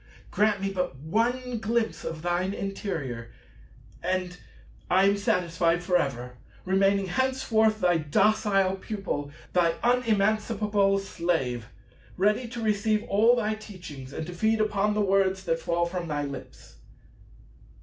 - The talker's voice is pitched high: Yes, high, 195 Hz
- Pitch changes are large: No, average, 3.9 semitones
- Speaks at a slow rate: Yes, slow, 130 wpm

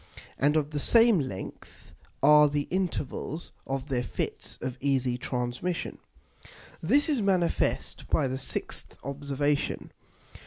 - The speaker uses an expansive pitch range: No, average, 4.5 semitones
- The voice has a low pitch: No, medium, 145 Hz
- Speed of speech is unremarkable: No, slow, 120 wpm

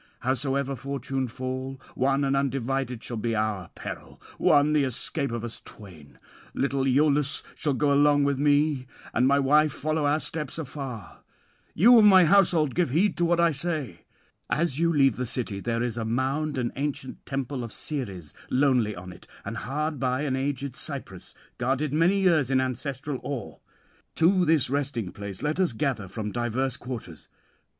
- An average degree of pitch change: Yes, average, 3.5 semitones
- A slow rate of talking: No, average, 170 wpm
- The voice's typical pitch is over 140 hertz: No, low, 135 Hz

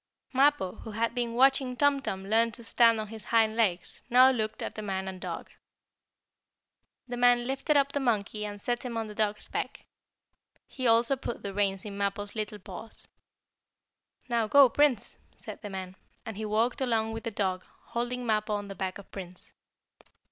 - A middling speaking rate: Yes, average, 185 wpm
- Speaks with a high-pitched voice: Yes, high, 225 Hz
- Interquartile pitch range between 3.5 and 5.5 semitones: No, average, 3.1 semitones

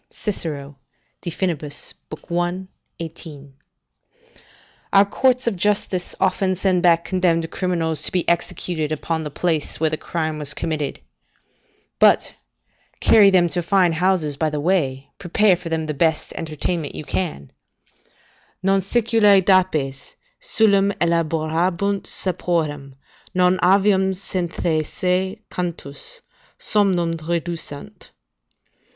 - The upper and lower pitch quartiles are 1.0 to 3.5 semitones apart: Yes, average, 3.2 semitones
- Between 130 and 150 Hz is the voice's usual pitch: No, medium, 175 Hz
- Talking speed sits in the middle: No, slow, 110 wpm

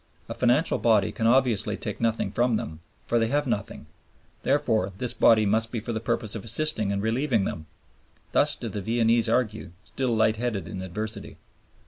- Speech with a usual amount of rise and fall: No, narrow, 2.2 semitones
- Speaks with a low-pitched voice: Yes, low, 115 Hz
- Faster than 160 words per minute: Yes, average, 180 wpm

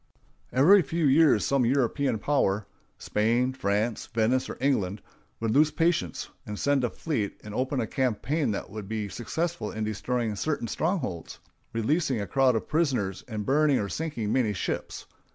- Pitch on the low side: Yes, low, 125 Hz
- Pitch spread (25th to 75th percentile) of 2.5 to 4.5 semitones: No, average, 5.2 semitones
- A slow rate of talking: No, average, 150 wpm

